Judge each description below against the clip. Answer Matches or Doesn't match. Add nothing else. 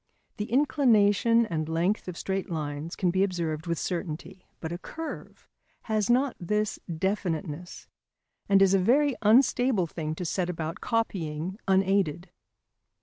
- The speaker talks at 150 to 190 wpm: Doesn't match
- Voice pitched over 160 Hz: Matches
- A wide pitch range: Doesn't match